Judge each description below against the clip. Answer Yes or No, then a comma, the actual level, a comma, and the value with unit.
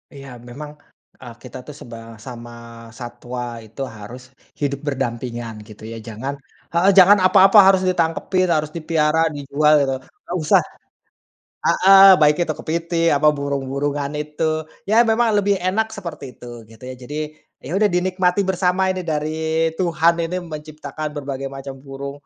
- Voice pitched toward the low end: No, medium, 150 Hz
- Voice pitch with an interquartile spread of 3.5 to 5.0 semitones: Yes, average, 4.6 semitones